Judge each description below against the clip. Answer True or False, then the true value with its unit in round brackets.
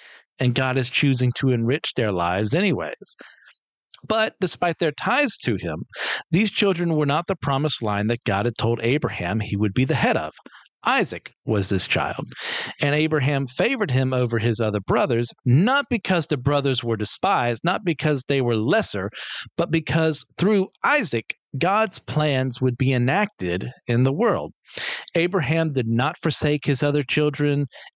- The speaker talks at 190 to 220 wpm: False (160 wpm)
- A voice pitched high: False (140 Hz)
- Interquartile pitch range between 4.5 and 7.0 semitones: True (5.2 semitones)